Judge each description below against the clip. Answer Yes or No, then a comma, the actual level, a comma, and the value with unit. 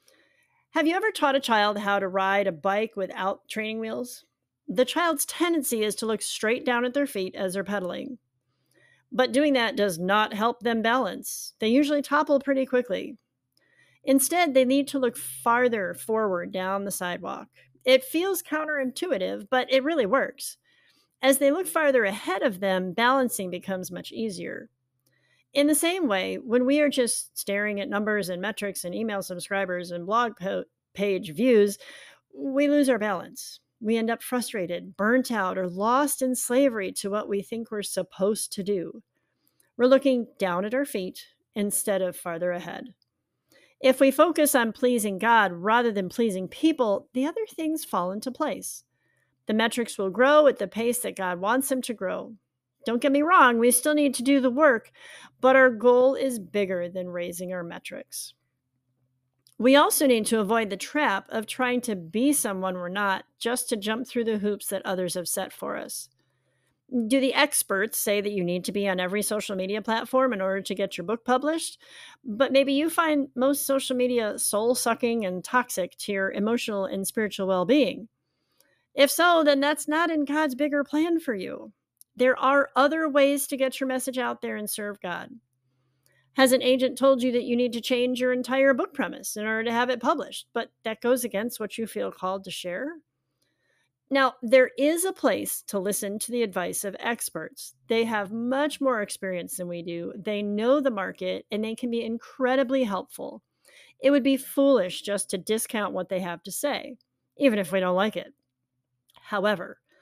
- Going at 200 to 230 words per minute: No, average, 185 wpm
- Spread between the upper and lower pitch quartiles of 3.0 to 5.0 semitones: No, wide, 5.5 semitones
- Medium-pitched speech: No, high, 230 Hz